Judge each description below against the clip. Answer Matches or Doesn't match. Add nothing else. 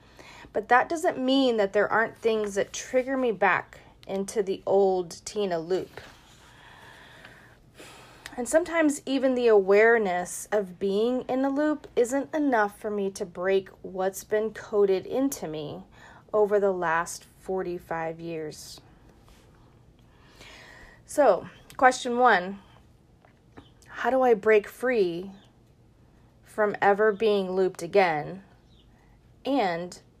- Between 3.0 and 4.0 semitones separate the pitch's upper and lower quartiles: Doesn't match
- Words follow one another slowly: Matches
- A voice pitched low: Doesn't match